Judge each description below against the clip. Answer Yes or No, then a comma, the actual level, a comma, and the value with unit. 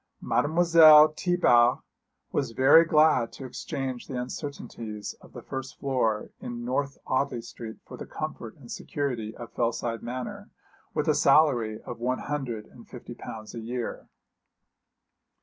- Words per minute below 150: Yes, average, 140 wpm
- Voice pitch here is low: Yes, low, 125 Hz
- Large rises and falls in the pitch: No, average, 3.5 semitones